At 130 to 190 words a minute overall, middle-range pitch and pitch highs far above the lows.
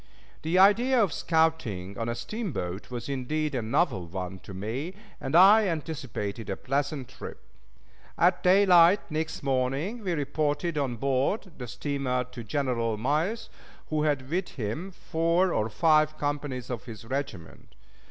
Yes: average, 145 wpm; medium, 145 Hz; wide, 5.8 semitones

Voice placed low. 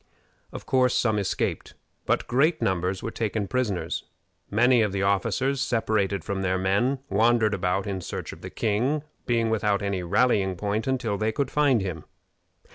Yes: low, 110 Hz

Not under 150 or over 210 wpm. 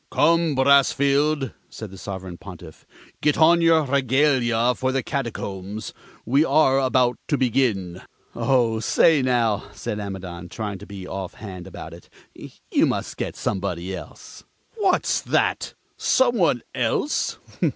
No: slow, 135 wpm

